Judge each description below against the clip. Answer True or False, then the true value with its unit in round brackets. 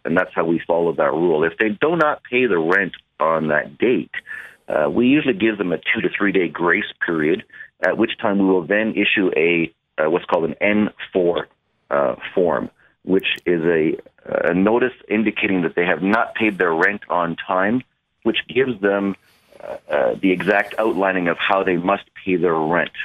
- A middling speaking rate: True (195 wpm)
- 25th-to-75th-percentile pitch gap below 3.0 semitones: False (3.7 semitones)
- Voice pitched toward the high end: False (100 Hz)